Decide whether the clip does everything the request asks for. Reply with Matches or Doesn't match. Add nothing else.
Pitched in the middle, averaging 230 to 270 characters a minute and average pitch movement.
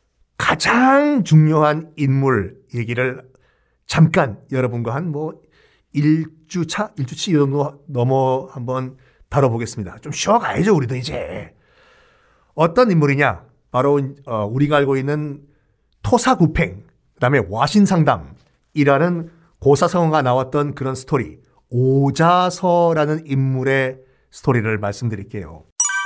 Matches